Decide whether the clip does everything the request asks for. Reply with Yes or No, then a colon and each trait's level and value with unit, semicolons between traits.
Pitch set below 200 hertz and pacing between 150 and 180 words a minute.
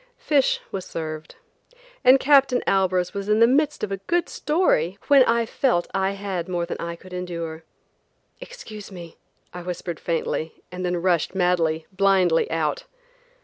Yes: medium, 185 Hz; average, 155 wpm